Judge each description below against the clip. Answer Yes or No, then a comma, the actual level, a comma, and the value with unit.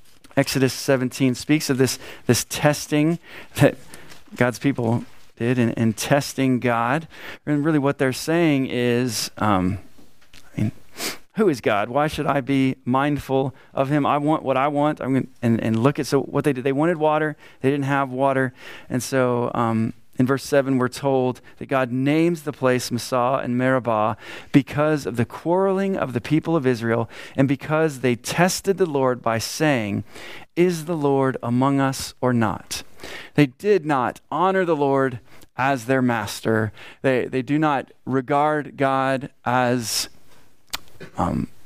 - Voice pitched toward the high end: No, low, 135 Hz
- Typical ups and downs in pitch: Yes, average, 3.3 semitones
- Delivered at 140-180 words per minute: Yes, average, 165 wpm